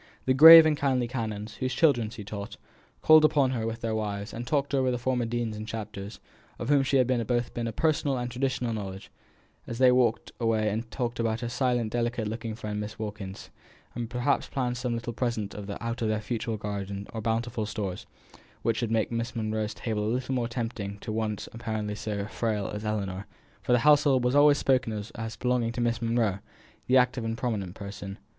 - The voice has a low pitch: Yes, low, 115 Hz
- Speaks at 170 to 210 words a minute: Yes, fast, 205 wpm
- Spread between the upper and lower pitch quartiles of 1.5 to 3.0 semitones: Yes, narrow, 2.6 semitones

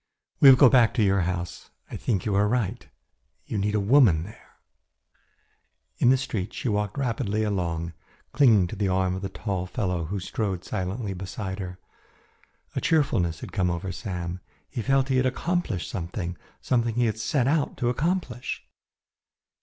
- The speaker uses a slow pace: No, average, 170 wpm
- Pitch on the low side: Yes, low, 105 Hz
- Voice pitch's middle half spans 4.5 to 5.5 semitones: Yes, average, 5.1 semitones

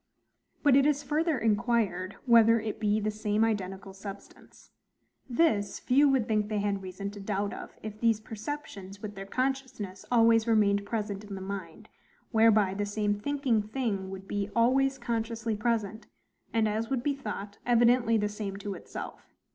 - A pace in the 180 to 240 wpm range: No, average, 165 wpm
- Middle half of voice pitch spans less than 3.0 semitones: Yes, narrow, 2.6 semitones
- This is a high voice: Yes, high, 215 Hz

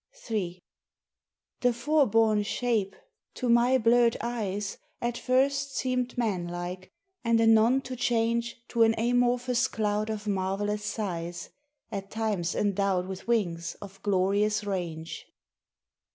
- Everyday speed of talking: No, slow, 125 wpm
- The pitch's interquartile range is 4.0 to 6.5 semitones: No, average, 3.5 semitones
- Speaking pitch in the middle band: No, high, 220 Hz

